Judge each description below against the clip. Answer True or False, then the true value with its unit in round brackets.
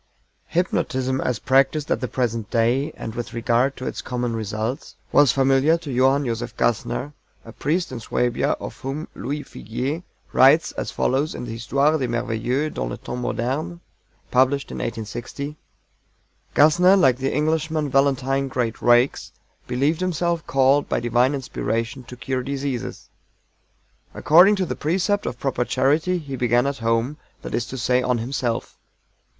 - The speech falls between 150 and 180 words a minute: True (155 wpm)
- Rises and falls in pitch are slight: False (3.3 semitones)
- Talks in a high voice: False (130 Hz)